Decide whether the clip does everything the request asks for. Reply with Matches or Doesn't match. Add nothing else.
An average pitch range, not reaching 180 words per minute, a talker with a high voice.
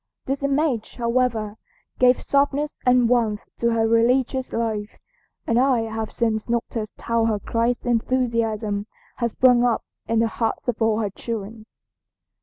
Doesn't match